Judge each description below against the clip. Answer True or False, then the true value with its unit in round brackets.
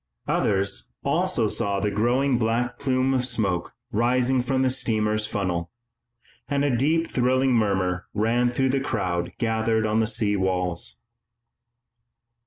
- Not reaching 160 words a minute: True (135 wpm)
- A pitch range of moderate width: True (4.0 semitones)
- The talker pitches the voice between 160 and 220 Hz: False (115 Hz)